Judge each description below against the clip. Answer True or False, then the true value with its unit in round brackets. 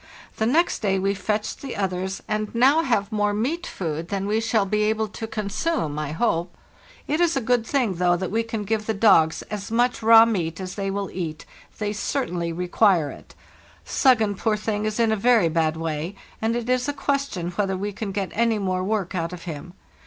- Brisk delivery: True (210 wpm)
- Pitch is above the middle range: True (205 Hz)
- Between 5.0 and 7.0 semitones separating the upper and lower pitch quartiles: False (3.7 semitones)